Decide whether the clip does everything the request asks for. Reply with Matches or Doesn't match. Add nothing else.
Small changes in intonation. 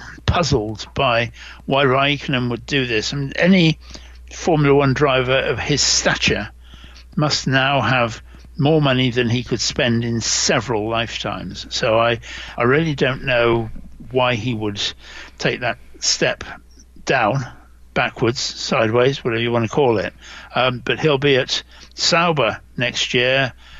Doesn't match